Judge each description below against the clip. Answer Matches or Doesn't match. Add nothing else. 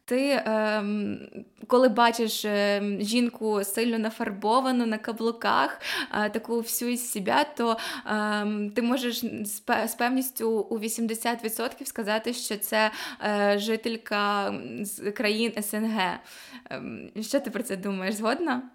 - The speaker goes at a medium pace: Doesn't match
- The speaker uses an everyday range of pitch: Doesn't match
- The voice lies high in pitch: Matches